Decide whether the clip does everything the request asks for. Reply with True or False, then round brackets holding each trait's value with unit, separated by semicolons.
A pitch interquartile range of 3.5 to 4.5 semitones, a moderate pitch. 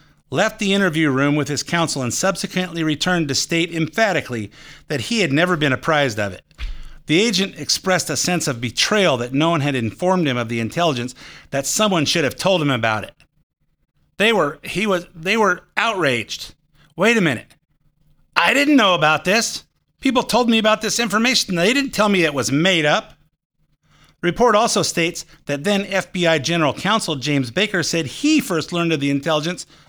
False (5.2 semitones; 165 Hz)